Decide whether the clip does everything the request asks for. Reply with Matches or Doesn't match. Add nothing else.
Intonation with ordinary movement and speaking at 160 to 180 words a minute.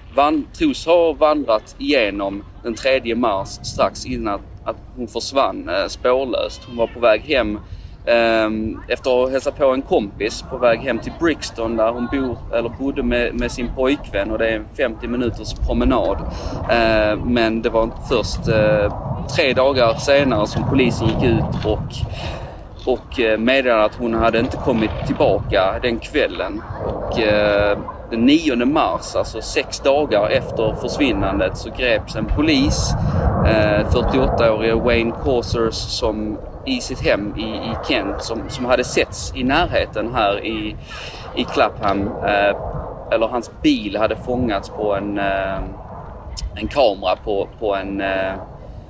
Doesn't match